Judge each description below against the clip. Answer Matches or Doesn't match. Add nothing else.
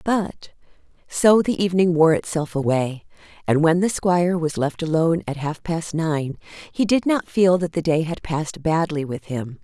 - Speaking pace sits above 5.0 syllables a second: Doesn't match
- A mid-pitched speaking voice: Matches